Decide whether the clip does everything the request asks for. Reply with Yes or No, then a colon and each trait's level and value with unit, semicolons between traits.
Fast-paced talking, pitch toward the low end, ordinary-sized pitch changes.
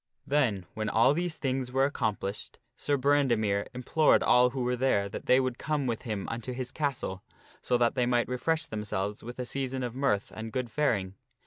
Yes: fast, 210 wpm; low, 125 Hz; average, 3.6 semitones